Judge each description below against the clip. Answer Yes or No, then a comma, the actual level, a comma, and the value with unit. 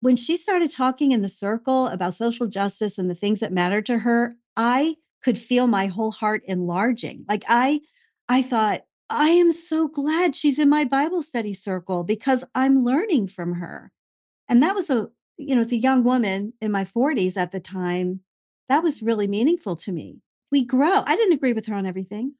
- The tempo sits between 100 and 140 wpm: No, average, 200 wpm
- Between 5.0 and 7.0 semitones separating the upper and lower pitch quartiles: Yes, wide, 5.5 semitones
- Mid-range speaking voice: No, high, 235 Hz